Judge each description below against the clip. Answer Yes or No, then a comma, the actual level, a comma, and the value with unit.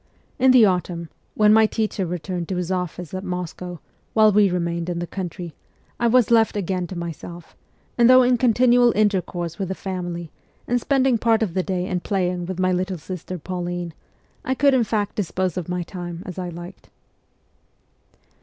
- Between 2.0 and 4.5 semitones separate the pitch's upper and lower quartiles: Yes, average, 3.5 semitones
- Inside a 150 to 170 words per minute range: No, average, 180 wpm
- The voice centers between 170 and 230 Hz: Yes, medium, 185 Hz